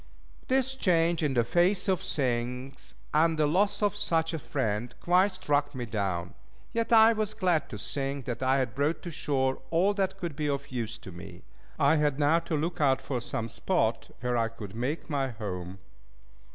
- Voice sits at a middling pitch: Yes, medium, 145 Hz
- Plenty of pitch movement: Yes, wide, 6.1 semitones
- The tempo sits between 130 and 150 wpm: No, average, 190 wpm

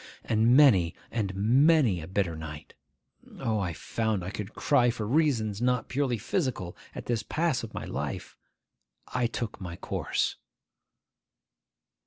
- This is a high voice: No, low, 110 Hz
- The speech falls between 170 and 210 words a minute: No, average, 140 wpm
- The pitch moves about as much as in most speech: Yes, average, 4.6 semitones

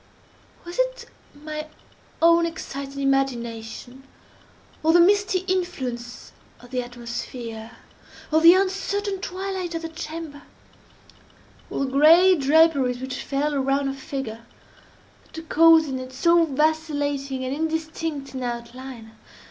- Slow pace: Yes, slow, 110 wpm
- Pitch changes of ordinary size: Yes, average, 4.2 semitones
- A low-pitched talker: No, very high, 290 Hz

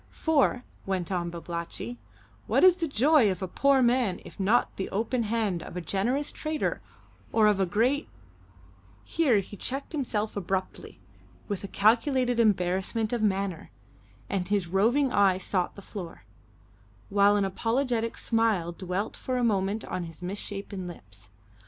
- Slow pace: No, average, 155 wpm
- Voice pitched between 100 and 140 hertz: No, high, 205 Hz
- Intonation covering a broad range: No, average, 4.6 semitones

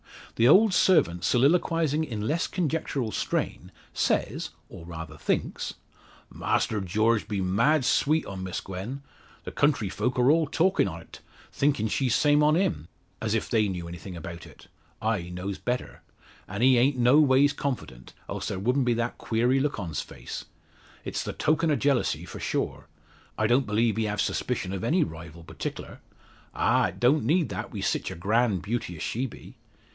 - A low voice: Yes, low, 115 Hz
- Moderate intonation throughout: No, wide, 6.8 semitones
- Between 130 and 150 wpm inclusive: No, average, 175 wpm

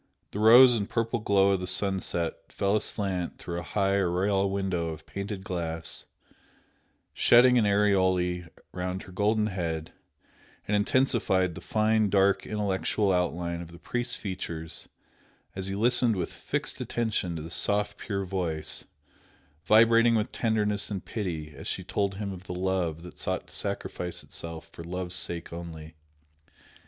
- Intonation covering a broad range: No, average, 3.0 semitones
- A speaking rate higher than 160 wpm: No, average, 150 wpm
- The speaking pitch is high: No, very low, 95 Hz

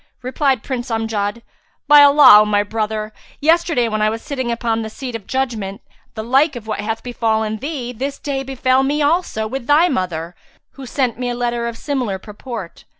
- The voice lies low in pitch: No, high, 240 Hz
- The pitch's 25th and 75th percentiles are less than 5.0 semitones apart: Yes, average, 3.7 semitones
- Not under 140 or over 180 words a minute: No, average, 190 wpm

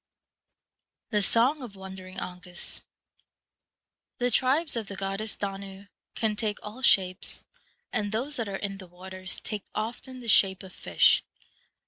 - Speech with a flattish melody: No, average, 3.2 semitones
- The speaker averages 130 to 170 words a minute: Yes, average, 140 wpm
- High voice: Yes, high, 200 Hz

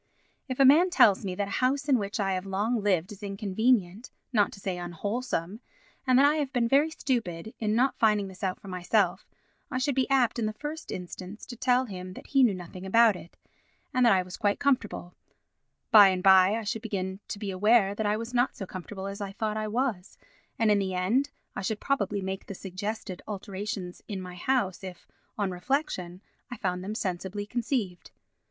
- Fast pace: Yes, fast, 210 wpm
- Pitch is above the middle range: Yes, high, 205 Hz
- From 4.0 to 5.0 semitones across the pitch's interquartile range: Yes, average, 4.3 semitones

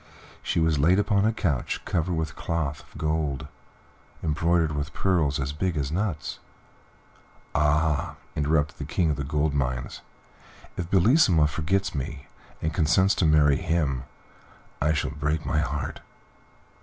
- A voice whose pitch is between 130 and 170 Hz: No, very low, 75 Hz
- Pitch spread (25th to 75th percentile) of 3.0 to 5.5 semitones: No, narrow, 2.6 semitones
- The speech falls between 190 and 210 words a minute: No, average, 145 wpm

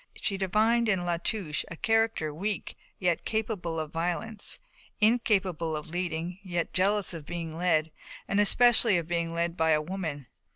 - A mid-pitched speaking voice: Yes, medium, 175 Hz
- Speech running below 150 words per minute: No, average, 160 wpm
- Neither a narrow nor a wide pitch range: Yes, average, 4.1 semitones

